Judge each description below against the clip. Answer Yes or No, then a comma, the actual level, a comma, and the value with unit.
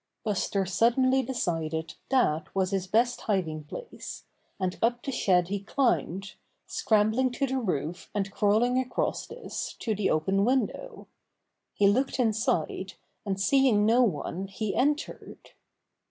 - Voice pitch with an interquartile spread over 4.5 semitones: Yes, average, 4.9 semitones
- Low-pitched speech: No, high, 210 Hz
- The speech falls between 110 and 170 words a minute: Yes, slow, 135 wpm